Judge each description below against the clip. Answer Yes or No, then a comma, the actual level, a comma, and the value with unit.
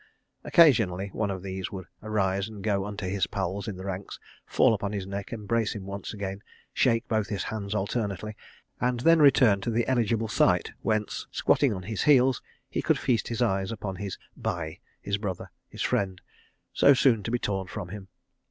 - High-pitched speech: No, low, 100 Hz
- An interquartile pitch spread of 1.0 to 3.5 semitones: Yes, average, 2.9 semitones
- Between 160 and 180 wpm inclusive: No, average, 190 wpm